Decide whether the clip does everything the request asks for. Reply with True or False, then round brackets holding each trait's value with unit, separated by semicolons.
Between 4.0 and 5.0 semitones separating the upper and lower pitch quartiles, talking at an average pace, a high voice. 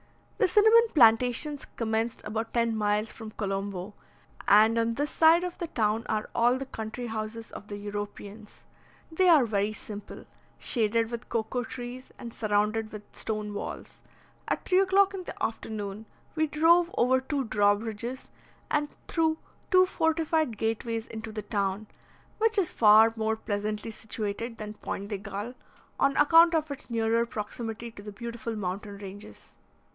True (4.3 semitones; 155 wpm; 225 Hz)